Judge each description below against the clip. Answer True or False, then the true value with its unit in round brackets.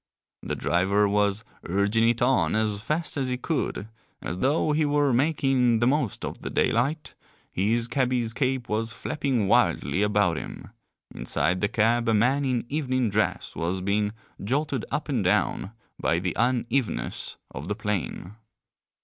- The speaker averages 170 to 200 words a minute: False (155 wpm)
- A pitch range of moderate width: True (4.5 semitones)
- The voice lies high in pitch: False (115 Hz)